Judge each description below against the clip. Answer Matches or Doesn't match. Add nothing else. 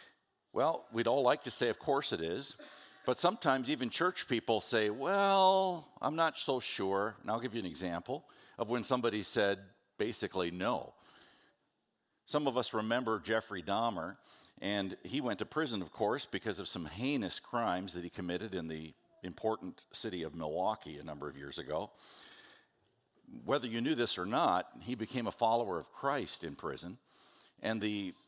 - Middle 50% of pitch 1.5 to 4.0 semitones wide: Doesn't match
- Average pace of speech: Matches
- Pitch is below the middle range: Matches